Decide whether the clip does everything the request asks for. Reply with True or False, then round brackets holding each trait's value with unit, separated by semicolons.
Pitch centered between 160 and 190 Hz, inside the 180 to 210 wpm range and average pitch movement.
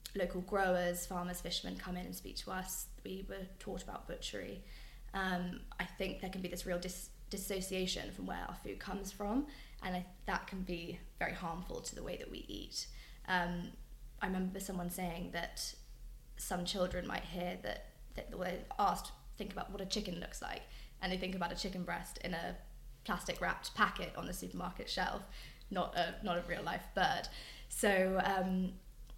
False (185 Hz; 190 wpm; 1.3 semitones)